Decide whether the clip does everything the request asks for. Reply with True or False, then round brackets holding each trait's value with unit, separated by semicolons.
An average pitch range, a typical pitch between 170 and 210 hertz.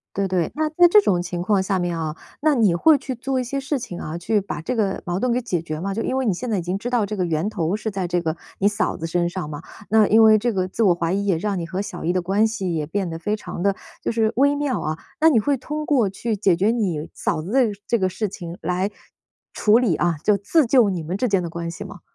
True (4.9 semitones; 195 Hz)